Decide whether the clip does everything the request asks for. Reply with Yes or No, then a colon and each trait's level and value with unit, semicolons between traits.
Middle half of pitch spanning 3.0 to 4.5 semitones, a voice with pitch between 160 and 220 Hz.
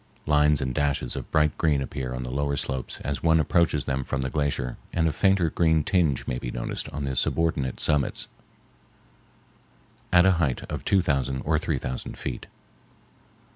No: average, 3.5 semitones; very low, 70 Hz